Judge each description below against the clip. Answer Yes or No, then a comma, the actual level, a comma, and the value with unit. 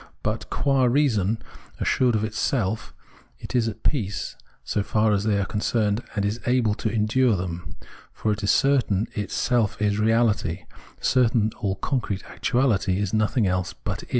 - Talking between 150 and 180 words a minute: Yes, average, 170 wpm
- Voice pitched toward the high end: No, low, 110 Hz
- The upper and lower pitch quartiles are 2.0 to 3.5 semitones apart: Yes, average, 2.9 semitones